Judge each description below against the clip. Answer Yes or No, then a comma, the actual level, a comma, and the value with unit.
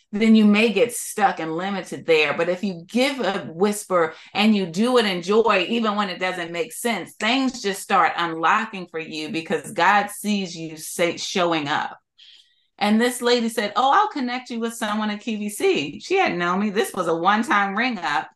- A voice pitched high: Yes, high, 210 Hz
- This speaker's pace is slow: No, fast, 205 wpm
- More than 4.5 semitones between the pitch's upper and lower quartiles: Yes, average, 5.0 semitones